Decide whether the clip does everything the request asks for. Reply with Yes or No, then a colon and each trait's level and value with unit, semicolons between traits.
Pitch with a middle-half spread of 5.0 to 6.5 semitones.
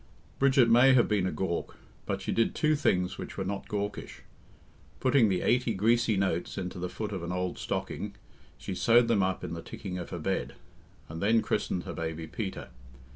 No: average, 4.3 semitones